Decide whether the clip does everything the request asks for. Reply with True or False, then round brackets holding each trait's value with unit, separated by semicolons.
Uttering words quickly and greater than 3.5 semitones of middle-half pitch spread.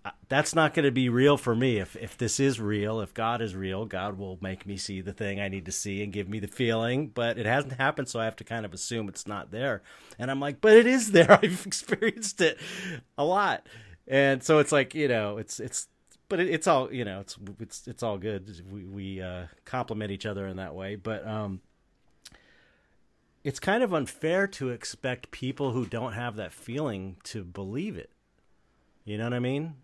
True (220 wpm; 5.5 semitones)